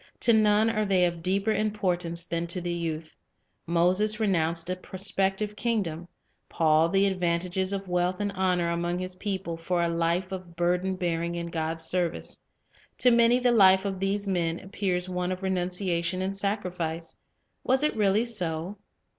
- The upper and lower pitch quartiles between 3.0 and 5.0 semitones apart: No, narrow, 2.6 semitones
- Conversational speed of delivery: Yes, average, 165 wpm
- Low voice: No, medium, 185 Hz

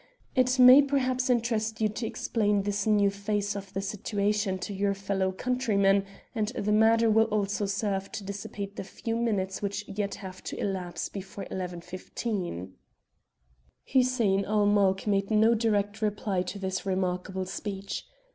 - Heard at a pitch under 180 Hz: No, high, 205 Hz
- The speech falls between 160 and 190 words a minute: No, average, 150 wpm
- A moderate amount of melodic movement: No, narrow, 2.1 semitones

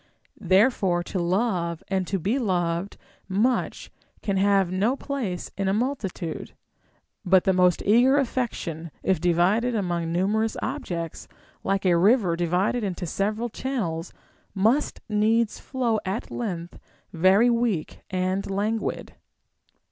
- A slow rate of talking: Yes, slow, 125 wpm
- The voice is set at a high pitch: Yes, high, 195 Hz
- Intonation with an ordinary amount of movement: Yes, average, 4.3 semitones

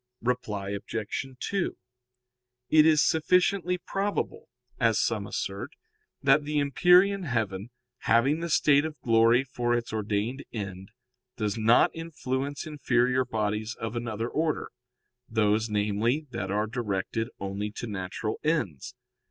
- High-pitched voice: No, low, 120 Hz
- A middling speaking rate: No, slow, 125 wpm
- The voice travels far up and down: Yes, wide, 6.0 semitones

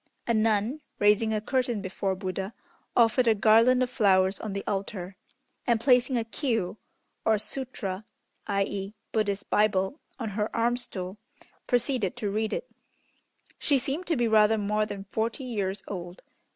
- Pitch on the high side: Yes, high, 215 Hz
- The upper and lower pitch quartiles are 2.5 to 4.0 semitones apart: Yes, average, 3.4 semitones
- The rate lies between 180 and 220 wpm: No, average, 150 wpm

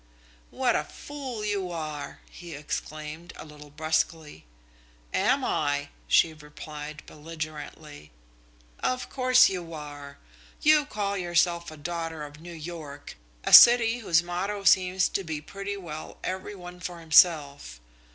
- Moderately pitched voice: Yes, medium, 165 Hz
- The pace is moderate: No, slow, 130 wpm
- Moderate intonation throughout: Yes, average, 4.0 semitones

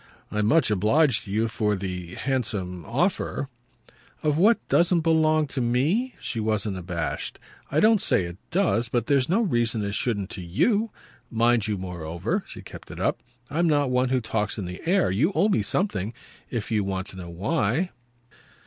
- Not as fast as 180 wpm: No, average, 185 wpm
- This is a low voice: Yes, low, 115 Hz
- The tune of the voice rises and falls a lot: Yes, wide, 7.9 semitones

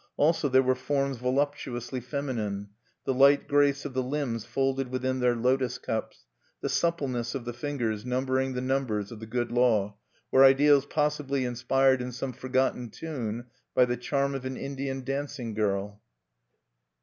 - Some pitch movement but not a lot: No, narrow, 2.3 semitones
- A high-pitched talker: No, low, 130 Hz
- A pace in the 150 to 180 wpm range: Yes, average, 160 wpm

